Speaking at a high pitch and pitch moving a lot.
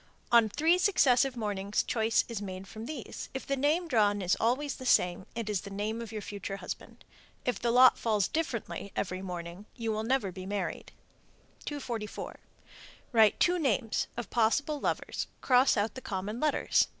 No: high, 225 Hz; average, 4.2 semitones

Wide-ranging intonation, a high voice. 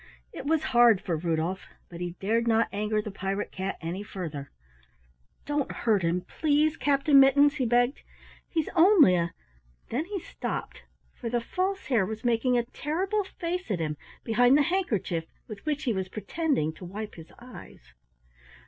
Yes: wide, 7.6 semitones; high, 230 Hz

